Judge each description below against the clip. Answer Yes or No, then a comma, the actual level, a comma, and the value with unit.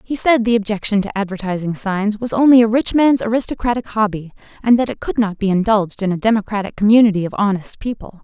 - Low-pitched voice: No, high, 215 Hz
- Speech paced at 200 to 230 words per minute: Yes, fast, 205 wpm